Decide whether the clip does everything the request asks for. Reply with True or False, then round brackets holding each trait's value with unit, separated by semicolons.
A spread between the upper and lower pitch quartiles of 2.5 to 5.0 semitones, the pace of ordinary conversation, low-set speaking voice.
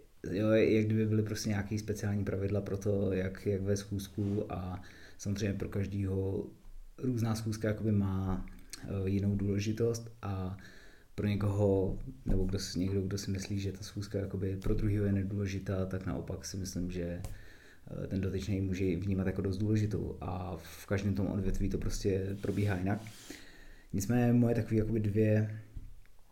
False (1.8 semitones; 155 wpm; 100 Hz)